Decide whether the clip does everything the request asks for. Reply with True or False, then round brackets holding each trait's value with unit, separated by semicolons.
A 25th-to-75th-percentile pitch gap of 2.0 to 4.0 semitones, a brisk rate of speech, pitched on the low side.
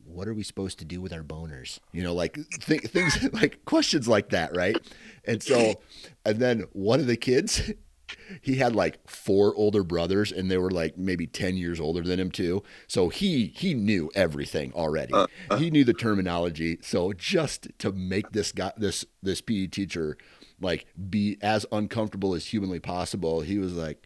False (3.7 semitones; 185 wpm; 95 Hz)